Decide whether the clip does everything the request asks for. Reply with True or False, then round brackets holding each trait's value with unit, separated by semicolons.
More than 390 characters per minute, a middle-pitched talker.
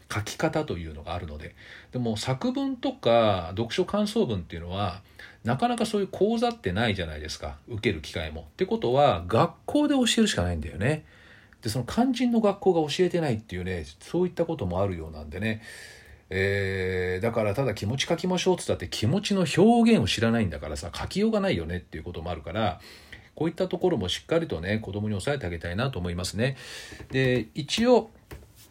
False (430 characters per minute; 115 Hz)